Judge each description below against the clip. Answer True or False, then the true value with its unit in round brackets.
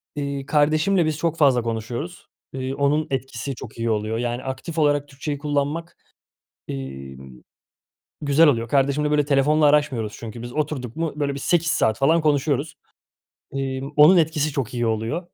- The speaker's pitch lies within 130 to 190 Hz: True (140 Hz)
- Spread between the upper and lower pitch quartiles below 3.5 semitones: False (3.8 semitones)